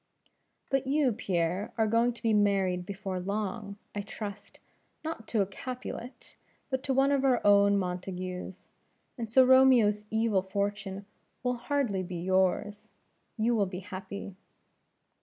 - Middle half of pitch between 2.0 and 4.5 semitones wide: Yes, average, 4.0 semitones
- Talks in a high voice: Yes, high, 205 Hz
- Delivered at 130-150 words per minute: Yes, average, 140 wpm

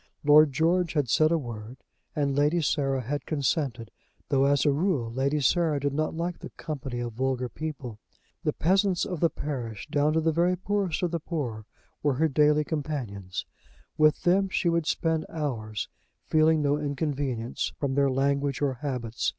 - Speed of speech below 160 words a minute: No, average, 175 wpm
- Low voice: No, medium, 145 Hz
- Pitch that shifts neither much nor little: Yes, average, 3.4 semitones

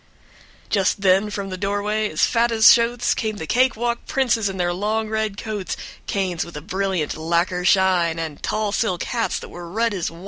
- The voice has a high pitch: Yes, high, 200 Hz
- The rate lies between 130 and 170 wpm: No, fast, 205 wpm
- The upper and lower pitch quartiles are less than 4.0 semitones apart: Yes, average, 3.5 semitones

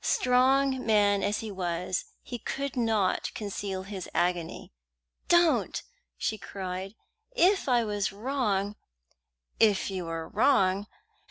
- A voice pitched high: Yes, high, 205 Hz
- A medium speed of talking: No, slow, 120 wpm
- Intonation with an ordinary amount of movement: Yes, average, 4.7 semitones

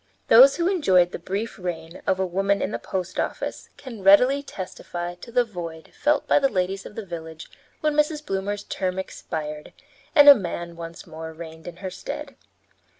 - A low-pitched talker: No, high, 190 Hz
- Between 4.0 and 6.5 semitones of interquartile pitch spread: Yes, average, 5.1 semitones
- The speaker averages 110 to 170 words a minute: No, average, 185 wpm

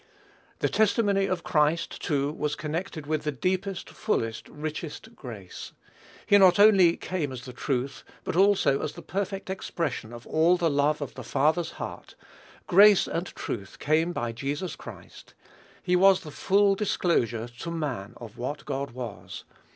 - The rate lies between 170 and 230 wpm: No, average, 160 wpm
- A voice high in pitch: No, medium, 155 Hz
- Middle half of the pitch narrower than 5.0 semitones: No, average, 5.3 semitones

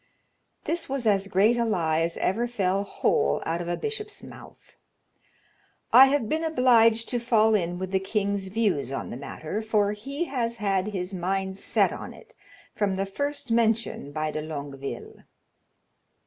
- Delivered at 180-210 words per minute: No, average, 165 wpm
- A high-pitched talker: Yes, high, 205 Hz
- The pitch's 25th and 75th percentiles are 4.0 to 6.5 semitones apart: Yes, average, 4.4 semitones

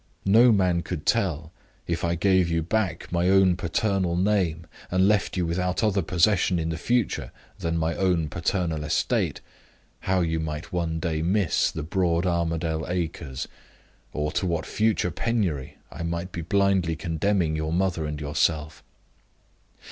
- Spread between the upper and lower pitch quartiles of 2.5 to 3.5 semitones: Yes, average, 2.8 semitones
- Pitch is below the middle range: Yes, very low, 85 Hz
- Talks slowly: No, average, 155 wpm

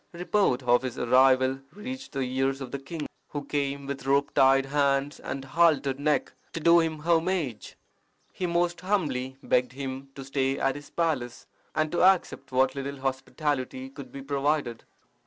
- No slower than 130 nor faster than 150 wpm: No, average, 165 wpm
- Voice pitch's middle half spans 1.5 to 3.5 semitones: Yes, average, 2.9 semitones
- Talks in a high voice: No, medium, 140 Hz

